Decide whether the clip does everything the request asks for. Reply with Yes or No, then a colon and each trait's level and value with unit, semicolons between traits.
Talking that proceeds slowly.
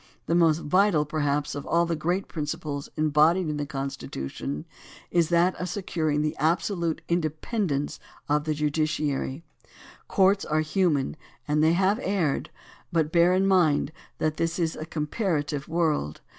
No: average, 145 wpm